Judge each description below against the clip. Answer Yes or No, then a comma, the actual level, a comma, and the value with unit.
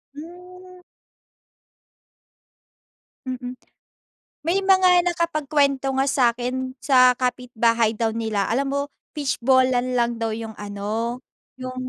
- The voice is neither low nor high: No, very high, 255 Hz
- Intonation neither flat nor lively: Yes, average, 3.6 semitones